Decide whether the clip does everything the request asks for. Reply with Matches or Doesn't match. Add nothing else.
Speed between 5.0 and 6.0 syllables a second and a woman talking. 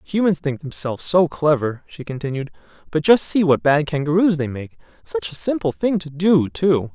Doesn't match